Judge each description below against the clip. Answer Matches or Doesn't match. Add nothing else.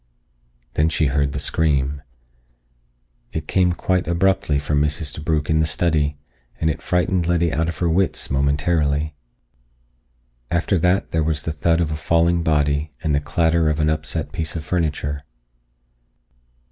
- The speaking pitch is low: Matches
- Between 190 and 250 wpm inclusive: Doesn't match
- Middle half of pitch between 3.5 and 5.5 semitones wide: Doesn't match